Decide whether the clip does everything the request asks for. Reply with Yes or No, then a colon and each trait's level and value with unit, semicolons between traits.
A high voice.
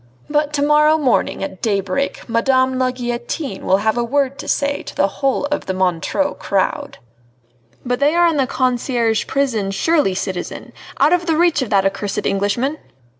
Yes: very high, 255 Hz